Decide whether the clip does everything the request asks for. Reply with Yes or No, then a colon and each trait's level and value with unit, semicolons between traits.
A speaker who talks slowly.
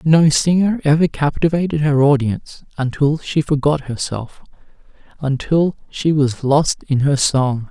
Yes: slow, 130 wpm